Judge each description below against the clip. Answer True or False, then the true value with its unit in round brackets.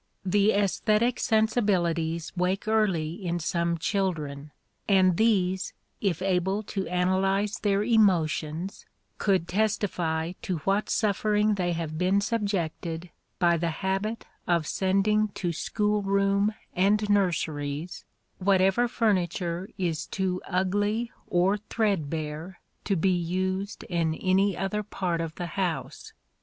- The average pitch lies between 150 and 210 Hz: True (190 Hz)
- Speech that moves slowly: True (120 wpm)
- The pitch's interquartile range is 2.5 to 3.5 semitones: True (3.1 semitones)